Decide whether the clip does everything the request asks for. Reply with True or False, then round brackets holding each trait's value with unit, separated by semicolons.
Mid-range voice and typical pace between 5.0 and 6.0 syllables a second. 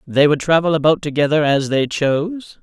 True (155 Hz; 5.2 syllables/s)